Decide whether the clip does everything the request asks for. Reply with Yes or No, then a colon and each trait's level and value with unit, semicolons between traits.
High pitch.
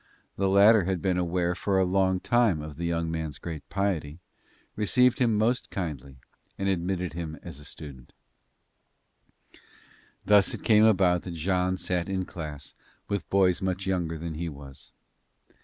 No: very low, 90 Hz